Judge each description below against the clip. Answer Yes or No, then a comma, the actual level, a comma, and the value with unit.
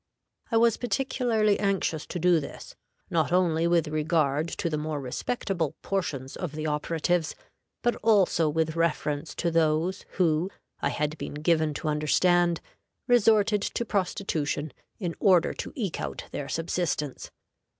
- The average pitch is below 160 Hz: No, medium, 170 Hz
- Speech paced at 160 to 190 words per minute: No, average, 140 wpm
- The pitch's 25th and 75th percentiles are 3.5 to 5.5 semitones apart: Yes, average, 4.1 semitones